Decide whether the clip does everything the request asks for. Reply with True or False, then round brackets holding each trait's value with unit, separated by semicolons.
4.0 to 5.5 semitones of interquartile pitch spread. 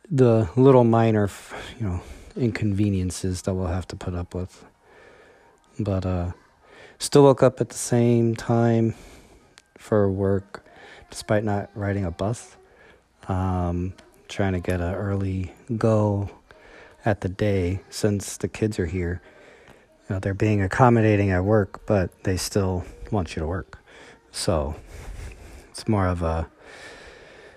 False (3.6 semitones)